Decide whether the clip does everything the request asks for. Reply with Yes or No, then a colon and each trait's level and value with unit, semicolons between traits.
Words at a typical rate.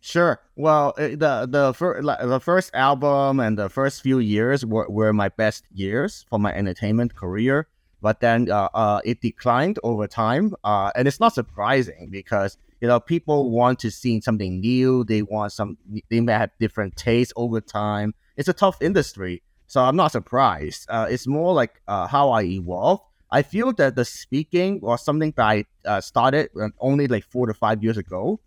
Yes: average, 185 wpm